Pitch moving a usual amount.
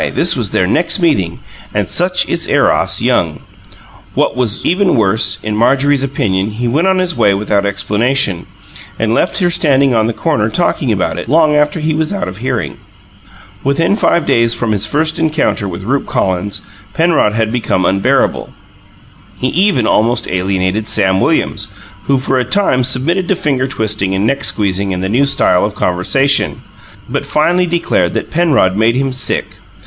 No: wide, 6.8 semitones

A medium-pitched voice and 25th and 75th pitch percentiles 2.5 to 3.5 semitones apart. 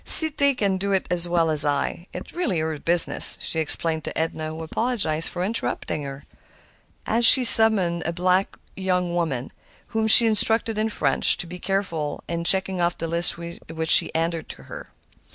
No: medium, 175 Hz; average, 4.0 semitones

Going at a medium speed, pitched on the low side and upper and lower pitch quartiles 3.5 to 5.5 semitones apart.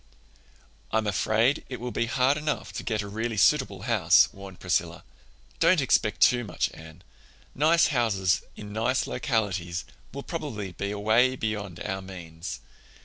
Yes: average, 145 wpm; low, 110 Hz; average, 4.5 semitones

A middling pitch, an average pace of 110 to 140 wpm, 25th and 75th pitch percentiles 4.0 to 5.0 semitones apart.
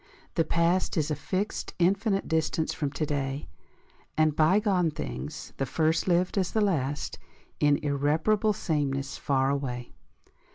Yes: medium, 155 Hz; slow, 135 wpm; average, 4.4 semitones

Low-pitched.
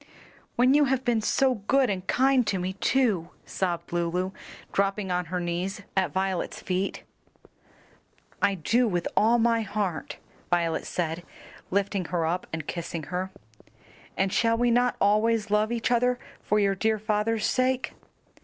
No: high, 200 Hz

